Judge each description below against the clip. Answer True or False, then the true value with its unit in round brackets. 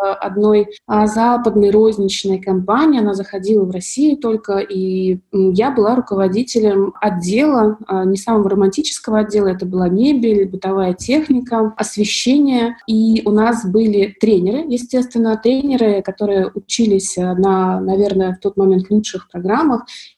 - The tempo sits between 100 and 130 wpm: True (120 wpm)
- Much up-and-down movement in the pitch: False (2.9 semitones)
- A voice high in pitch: True (210 Hz)